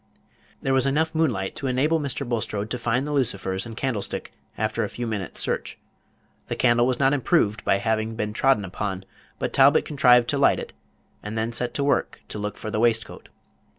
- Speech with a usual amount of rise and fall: Yes, average, 4.0 semitones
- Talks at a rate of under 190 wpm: No, average, 195 wpm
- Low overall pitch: Yes, low, 120 Hz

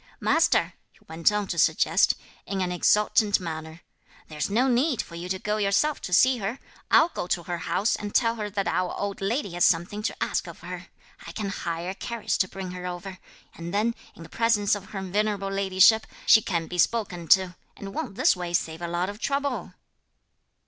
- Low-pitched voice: No, high, 195 Hz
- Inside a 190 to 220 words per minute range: Yes, fast, 205 wpm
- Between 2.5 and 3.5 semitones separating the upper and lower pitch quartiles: Yes, average, 3.1 semitones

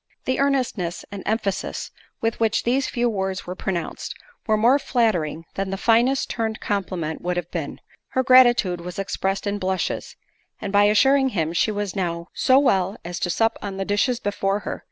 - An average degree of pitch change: Yes, average, 4.1 semitones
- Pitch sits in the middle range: No, high, 205 Hz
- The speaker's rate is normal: Yes, average, 180 wpm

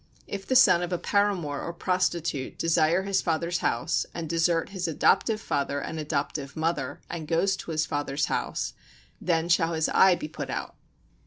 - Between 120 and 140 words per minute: No, average, 180 wpm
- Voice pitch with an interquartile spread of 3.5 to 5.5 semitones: No, average, 2.8 semitones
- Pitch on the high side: No, medium, 165 Hz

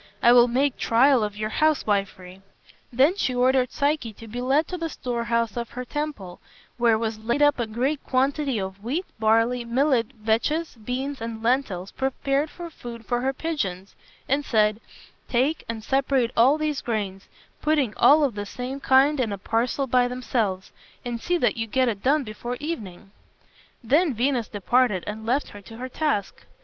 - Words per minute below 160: No, average, 175 wpm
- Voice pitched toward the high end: Yes, high, 245 Hz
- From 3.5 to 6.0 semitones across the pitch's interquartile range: Yes, average, 3.9 semitones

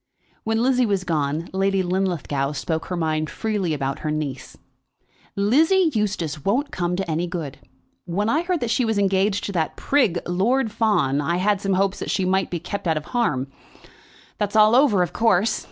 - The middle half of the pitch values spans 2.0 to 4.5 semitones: No, average, 5.0 semitones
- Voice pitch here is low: No, high, 190 Hz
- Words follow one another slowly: No, average, 185 wpm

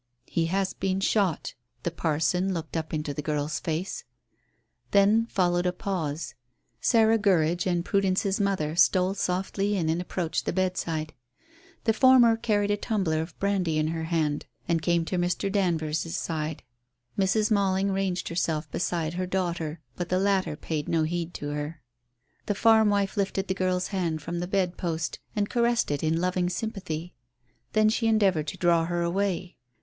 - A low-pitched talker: No, medium, 180 Hz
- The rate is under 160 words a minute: No, average, 165 wpm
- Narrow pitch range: No, average, 3.4 semitones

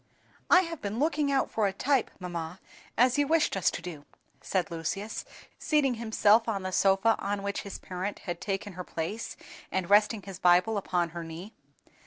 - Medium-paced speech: Yes, average, 185 wpm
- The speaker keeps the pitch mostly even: No, average, 4.1 semitones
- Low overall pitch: No, high, 200 Hz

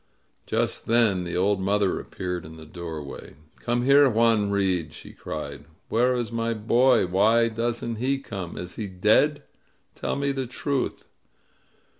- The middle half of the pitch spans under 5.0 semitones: Yes, average, 4.6 semitones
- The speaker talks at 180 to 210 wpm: No, average, 150 wpm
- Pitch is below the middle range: Yes, low, 110 Hz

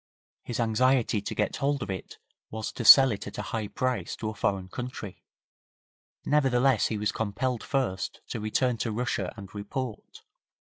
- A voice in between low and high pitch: No, low, 115 Hz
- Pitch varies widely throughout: No, average, 3.8 semitones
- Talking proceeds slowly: No, average, 170 wpm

